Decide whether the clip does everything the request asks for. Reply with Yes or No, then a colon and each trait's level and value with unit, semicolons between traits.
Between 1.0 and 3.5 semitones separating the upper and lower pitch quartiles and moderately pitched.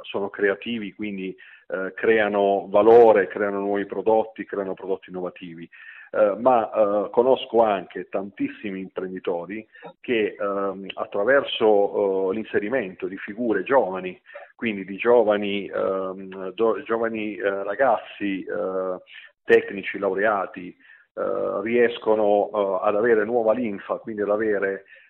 No: average, 2.8 semitones; low, 100 Hz